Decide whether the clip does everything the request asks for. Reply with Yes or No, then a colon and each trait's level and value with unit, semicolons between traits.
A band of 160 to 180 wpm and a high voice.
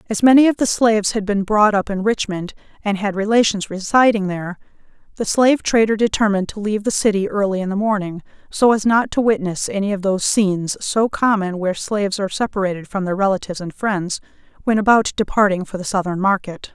No: average, 195 wpm; high, 205 Hz